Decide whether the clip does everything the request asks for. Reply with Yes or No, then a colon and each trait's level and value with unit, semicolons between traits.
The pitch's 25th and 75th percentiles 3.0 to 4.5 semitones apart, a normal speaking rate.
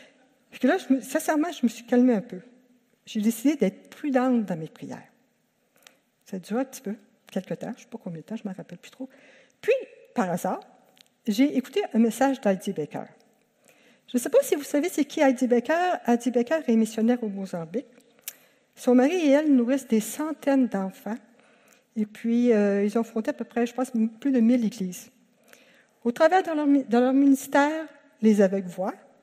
Yes: average, 3.8 semitones; average, 200 wpm